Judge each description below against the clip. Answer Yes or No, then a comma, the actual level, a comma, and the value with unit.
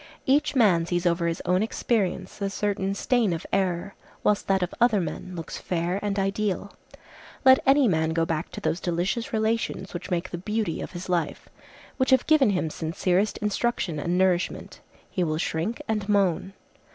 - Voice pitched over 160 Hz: Yes, high, 190 Hz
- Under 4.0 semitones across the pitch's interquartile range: Yes, average, 3.5 semitones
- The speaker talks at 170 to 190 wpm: Yes, average, 175 wpm